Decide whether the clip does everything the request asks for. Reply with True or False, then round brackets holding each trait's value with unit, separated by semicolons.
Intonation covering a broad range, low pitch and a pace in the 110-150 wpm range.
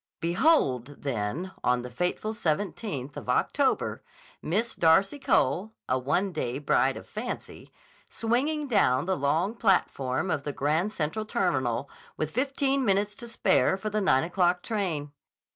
False (7.1 semitones; 180 Hz; 145 wpm)